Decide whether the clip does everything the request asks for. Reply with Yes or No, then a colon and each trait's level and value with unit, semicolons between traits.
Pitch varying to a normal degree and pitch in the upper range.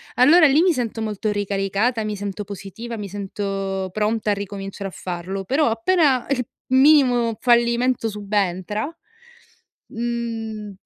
Yes: average, 3.4 semitones; high, 215 Hz